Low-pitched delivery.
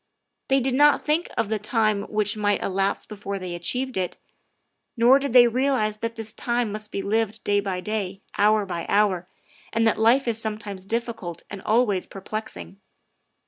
No: high, 215 Hz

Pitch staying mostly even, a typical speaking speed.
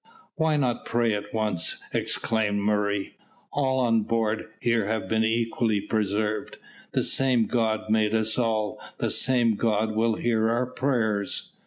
Yes: narrow, 1.8 semitones; average, 145 wpm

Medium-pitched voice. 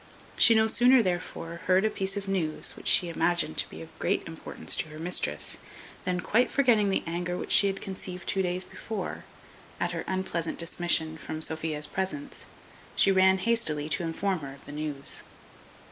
Yes: medium, 180 Hz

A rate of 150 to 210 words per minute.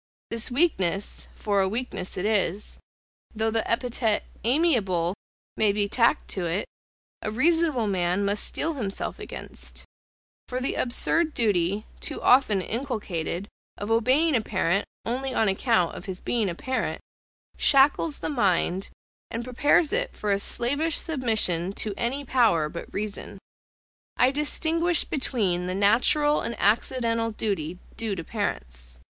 No: average, 140 wpm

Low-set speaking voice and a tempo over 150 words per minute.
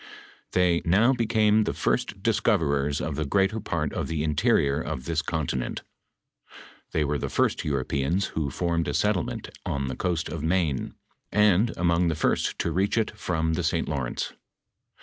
Yes: very low, 80 Hz; average, 165 wpm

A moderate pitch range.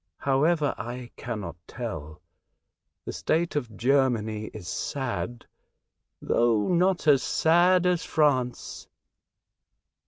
No: wide, 5.9 semitones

